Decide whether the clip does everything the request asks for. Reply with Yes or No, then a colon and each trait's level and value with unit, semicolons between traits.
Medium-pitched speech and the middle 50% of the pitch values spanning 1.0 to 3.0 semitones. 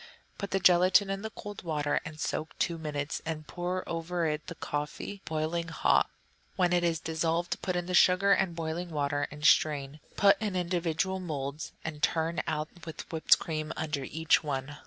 Yes: medium, 165 Hz; average, 2.7 semitones